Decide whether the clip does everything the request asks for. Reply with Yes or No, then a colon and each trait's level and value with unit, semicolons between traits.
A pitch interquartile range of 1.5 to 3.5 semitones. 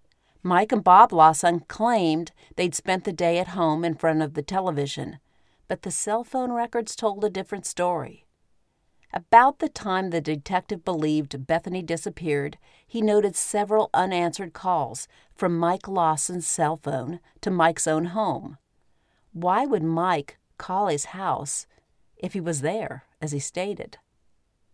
No: average, 4.3 semitones